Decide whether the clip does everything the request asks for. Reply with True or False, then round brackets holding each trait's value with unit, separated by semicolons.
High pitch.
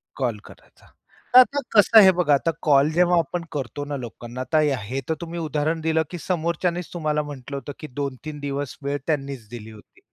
False (150 Hz)